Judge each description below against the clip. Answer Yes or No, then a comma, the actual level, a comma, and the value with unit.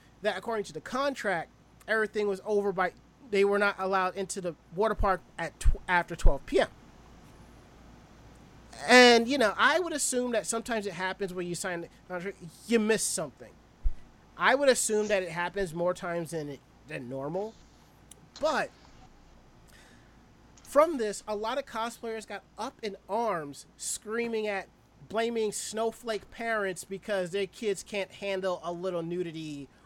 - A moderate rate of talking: Yes, average, 150 wpm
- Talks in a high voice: Yes, high, 200 Hz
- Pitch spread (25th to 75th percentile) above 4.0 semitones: No, average, 3.7 semitones